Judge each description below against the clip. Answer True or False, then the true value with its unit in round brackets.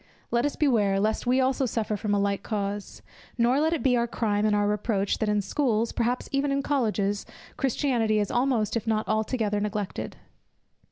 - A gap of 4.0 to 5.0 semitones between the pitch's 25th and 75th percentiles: False (3.5 semitones)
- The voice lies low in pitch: False (220 Hz)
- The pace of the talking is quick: False (185 wpm)